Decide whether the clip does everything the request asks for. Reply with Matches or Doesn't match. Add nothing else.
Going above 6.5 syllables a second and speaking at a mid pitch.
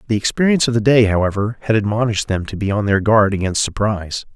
Doesn't match